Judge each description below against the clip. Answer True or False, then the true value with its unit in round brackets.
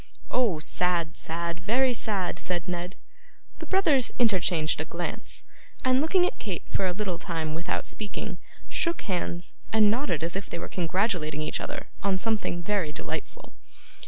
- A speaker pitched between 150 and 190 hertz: True (185 Hz)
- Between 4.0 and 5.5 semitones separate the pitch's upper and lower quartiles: True (4.6 semitones)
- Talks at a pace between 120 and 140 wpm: False (160 wpm)